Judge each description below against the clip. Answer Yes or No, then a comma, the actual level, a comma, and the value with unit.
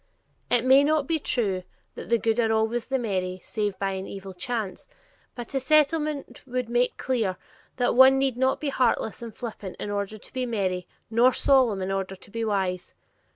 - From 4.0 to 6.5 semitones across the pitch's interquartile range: Yes, average, 4.8 semitones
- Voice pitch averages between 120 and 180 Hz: No, high, 230 Hz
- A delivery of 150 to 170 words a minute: No, average, 195 wpm